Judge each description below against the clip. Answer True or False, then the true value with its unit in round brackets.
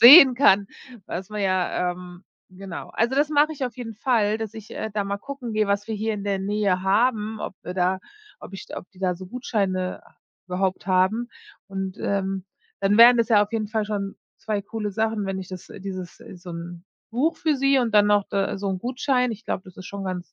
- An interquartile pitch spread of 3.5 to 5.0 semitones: False (3.1 semitones)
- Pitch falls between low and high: False (205 Hz)